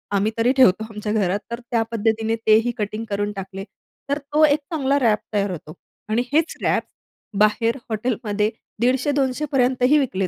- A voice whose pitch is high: Yes, high, 225 Hz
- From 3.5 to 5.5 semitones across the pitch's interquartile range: Yes, average, 3.9 semitones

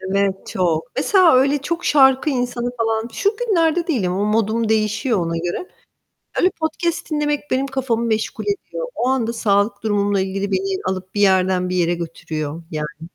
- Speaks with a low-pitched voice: No, high, 220 Hz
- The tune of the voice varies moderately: No, wide, 6.4 semitones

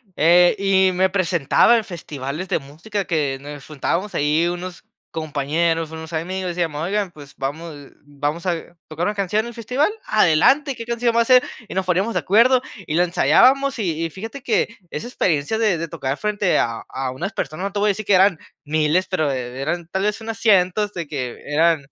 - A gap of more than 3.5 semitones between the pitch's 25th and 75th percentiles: Yes, average, 5.2 semitones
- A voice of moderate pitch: Yes, medium, 175 Hz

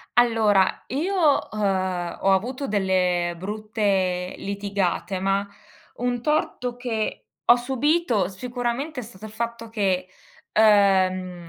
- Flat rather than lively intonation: No, average, 4.4 semitones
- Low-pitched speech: No, high, 210 Hz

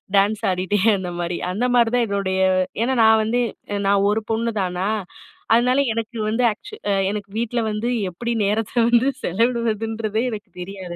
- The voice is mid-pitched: No, high, 220 Hz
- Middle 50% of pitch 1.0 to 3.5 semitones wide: Yes, average, 2.9 semitones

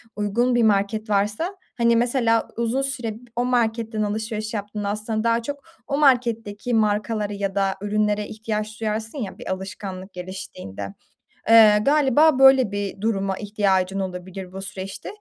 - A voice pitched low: No, high, 215 Hz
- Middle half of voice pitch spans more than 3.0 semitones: No, average, 2.7 semitones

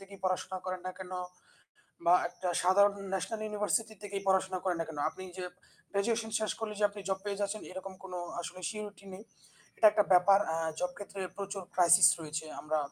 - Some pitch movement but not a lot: No, narrow, 2.0 semitones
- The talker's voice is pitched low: No, high, 190 Hz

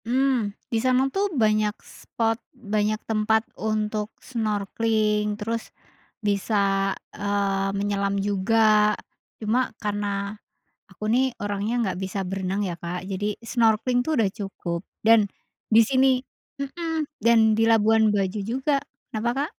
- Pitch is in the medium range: No, high, 215 Hz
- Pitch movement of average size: No, narrow, 2.1 semitones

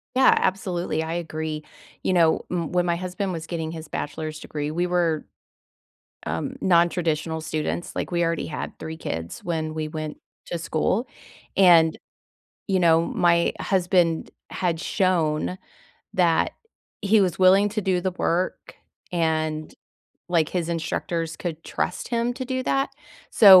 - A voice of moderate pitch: Yes, medium, 170 Hz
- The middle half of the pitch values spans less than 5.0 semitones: Yes, narrow, 2.5 semitones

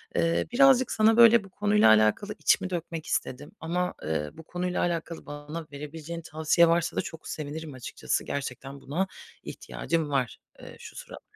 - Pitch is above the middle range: No, medium, 160 Hz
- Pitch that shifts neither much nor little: Yes, average, 4.1 semitones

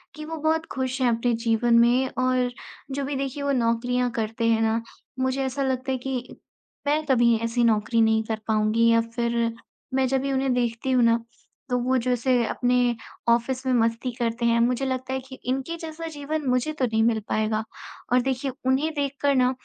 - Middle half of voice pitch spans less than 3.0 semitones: Yes, narrow, 2.4 semitones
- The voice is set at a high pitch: Yes, very high, 250 Hz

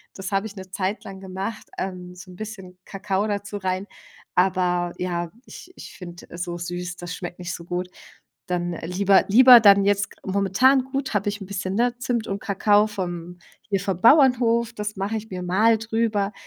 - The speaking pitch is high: Yes, high, 195 Hz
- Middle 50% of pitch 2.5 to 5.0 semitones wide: Yes, average, 2.9 semitones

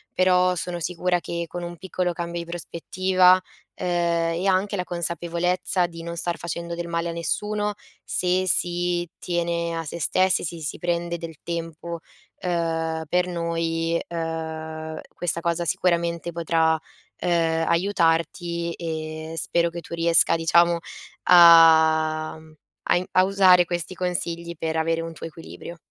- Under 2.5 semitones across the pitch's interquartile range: Yes, narrow, 1.2 semitones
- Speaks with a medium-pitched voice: Yes, medium, 170 Hz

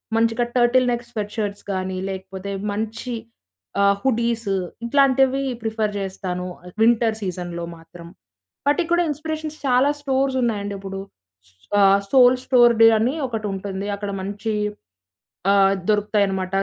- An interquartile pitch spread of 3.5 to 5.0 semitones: Yes, average, 4.1 semitones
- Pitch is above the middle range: Yes, high, 220 Hz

